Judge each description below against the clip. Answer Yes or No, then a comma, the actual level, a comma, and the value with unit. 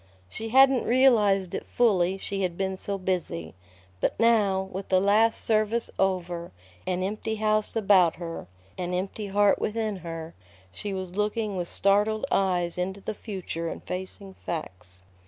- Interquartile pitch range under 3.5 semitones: Yes, average, 3.0 semitones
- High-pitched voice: Yes, high, 195 Hz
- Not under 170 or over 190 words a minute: No, average, 155 wpm